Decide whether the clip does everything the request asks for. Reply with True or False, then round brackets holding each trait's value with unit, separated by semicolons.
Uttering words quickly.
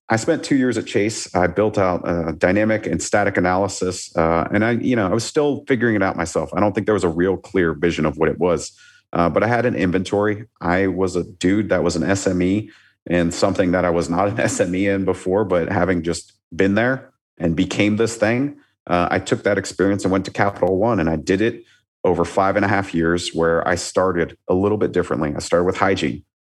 True (235 wpm)